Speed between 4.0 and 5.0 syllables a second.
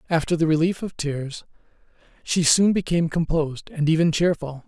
No: 5.4 syllables/s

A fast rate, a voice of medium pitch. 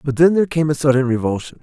Yes: fast, 260 wpm; medium, 145 Hz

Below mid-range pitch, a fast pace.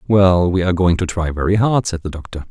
Yes: very low, 90 Hz; fast, 265 wpm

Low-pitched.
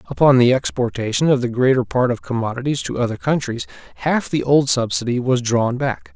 Yes: low, 130 Hz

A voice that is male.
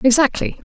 No: female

